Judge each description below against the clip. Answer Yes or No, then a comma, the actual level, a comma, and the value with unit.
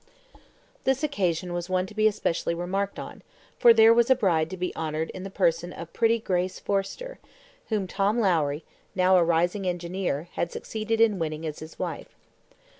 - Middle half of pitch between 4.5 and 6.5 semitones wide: No, average, 4.1 semitones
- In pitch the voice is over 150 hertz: Yes, medium, 185 Hz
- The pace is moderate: Yes, average, 180 wpm